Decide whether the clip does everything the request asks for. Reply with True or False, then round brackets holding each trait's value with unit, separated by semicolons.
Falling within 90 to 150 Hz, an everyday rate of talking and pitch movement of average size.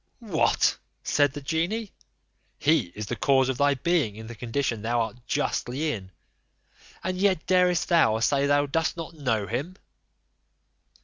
False (140 Hz; 150 wpm; 5.8 semitones)